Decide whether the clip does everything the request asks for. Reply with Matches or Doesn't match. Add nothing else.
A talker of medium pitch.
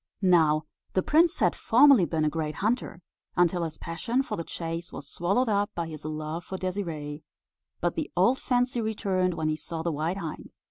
Matches